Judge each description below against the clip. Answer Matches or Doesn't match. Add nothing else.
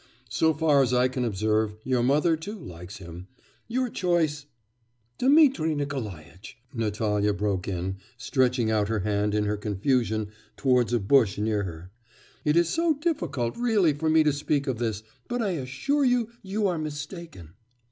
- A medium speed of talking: Matches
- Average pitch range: Doesn't match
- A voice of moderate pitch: Doesn't match